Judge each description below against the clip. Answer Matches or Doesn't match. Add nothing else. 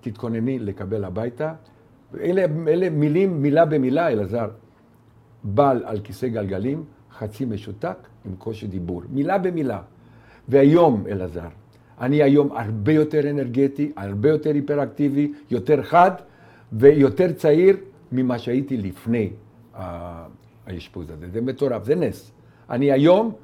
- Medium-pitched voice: Doesn't match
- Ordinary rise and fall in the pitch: Matches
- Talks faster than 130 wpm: Doesn't match